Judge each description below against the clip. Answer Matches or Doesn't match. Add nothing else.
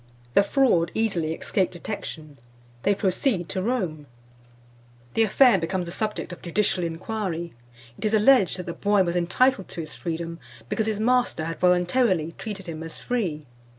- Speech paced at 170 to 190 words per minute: Doesn't match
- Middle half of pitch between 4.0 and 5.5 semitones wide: Matches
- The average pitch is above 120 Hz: Matches